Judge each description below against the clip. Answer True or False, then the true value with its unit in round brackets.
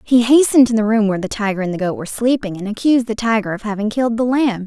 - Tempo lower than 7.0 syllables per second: False (7.2 syllables/s)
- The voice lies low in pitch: False (220 Hz)